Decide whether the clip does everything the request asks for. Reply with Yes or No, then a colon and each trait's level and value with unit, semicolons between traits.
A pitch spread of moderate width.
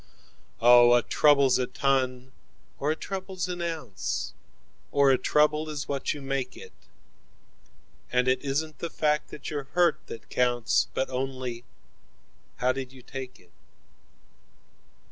Yes: average, 3.1 semitones